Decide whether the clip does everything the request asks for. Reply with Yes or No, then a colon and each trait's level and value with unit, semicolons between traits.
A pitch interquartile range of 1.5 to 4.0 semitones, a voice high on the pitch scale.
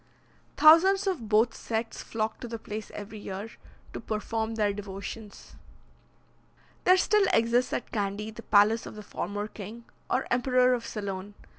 Yes: average, 2.9 semitones; high, 220 Hz